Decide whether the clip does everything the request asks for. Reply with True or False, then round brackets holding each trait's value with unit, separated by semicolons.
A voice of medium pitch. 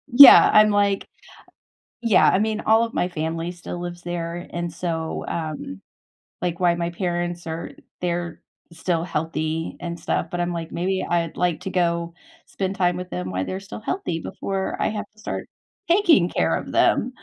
True (175 Hz)